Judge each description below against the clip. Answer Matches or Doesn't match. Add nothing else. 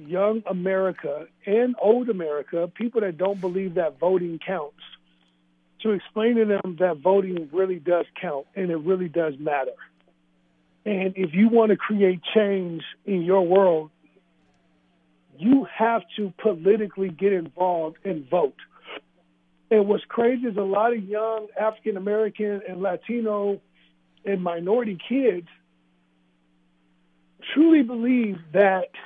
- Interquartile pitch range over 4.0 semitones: Matches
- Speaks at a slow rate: Matches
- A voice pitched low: Doesn't match